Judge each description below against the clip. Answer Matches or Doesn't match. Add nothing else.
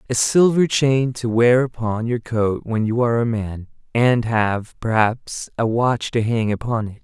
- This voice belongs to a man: Matches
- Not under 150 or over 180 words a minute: Doesn't match